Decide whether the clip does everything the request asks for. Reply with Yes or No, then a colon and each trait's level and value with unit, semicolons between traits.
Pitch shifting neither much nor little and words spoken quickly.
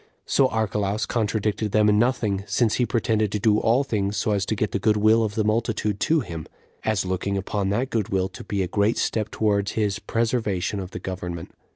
No: narrow, 2.0 semitones; fast, 215 wpm